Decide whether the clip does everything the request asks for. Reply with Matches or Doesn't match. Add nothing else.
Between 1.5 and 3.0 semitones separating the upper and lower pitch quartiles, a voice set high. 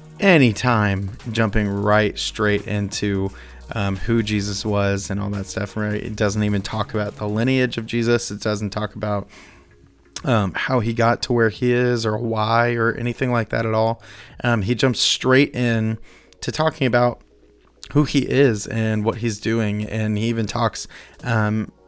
Doesn't match